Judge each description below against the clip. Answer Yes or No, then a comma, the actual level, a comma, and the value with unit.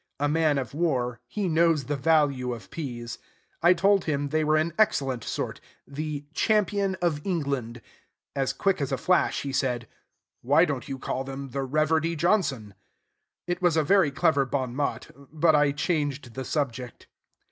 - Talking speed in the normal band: Yes, average, 170 wpm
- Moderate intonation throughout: Yes, average, 3.6 semitones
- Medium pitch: Yes, medium, 145 Hz